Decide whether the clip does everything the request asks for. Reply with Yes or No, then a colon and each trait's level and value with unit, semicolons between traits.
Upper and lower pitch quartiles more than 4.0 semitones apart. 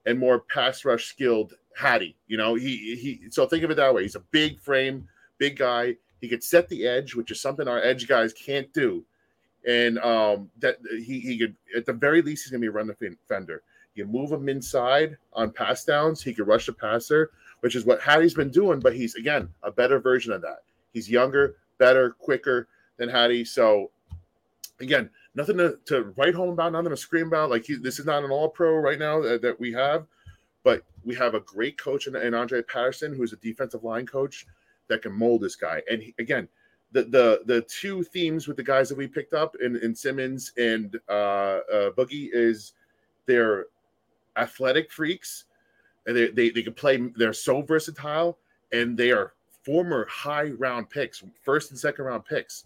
Yes: average, 4.5 semitones